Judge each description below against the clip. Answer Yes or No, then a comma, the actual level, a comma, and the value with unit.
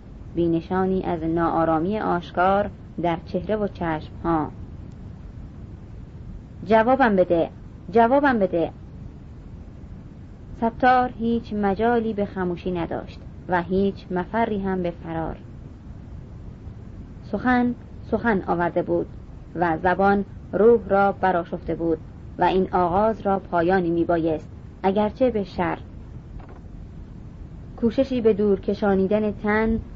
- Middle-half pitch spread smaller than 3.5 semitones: No, average, 4.3 semitones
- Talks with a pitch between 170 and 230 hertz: Yes, medium, 185 Hz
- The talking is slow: Yes, slow, 100 wpm